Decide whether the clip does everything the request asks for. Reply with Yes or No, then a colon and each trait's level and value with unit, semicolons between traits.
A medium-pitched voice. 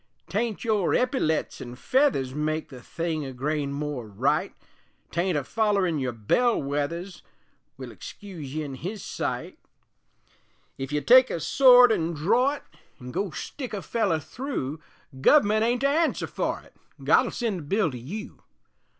Yes: medium, 170 Hz